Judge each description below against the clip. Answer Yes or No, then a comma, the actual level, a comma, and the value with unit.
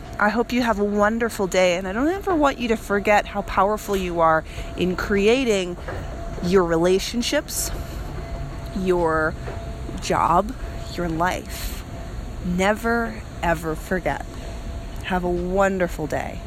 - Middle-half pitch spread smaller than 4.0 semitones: No, average, 4.5 semitones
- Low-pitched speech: No, medium, 185 Hz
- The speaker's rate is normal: No, slow, 125 wpm